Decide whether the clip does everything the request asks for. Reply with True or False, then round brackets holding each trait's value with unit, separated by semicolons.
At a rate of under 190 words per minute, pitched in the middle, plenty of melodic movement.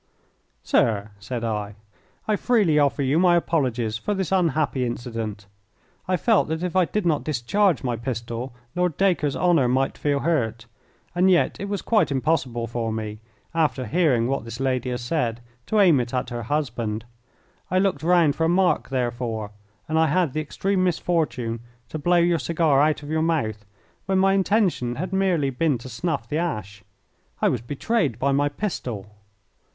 True (175 wpm; 145 Hz; 6.6 semitones)